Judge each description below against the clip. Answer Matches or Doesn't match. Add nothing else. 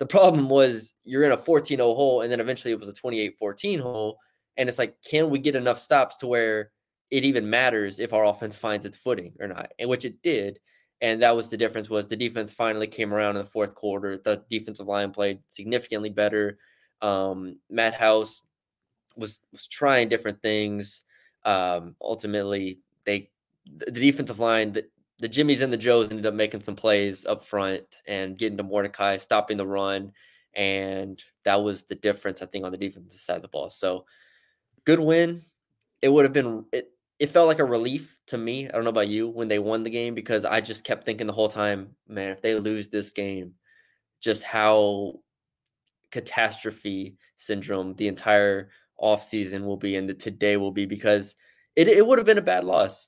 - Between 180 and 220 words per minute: Matches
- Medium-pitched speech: Doesn't match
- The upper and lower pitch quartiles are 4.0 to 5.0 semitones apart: Doesn't match